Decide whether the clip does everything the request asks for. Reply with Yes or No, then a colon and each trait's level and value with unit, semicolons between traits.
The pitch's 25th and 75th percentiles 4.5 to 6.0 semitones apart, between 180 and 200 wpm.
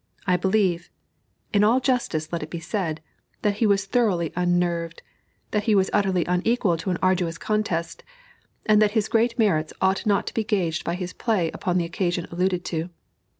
No: average, 3.6 semitones; average, 185 wpm